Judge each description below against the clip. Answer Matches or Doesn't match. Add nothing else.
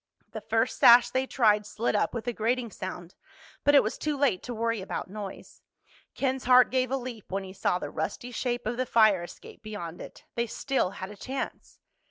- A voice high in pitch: Matches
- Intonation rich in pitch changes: Doesn't match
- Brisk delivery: Matches